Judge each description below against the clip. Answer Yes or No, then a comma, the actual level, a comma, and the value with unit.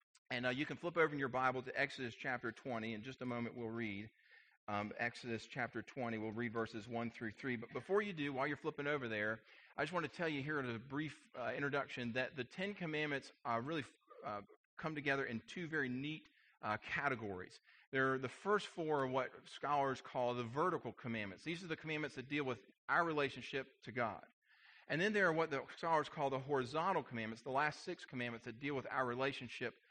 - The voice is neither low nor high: No, low, 130 Hz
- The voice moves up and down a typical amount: Yes, average, 4.1 semitones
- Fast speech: Yes, fast, 215 wpm